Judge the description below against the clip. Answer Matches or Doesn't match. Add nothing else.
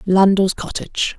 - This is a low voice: Doesn't match